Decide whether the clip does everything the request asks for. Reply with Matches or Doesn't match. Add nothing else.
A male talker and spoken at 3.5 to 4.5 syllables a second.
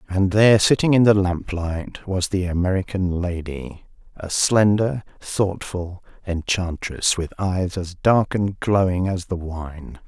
Matches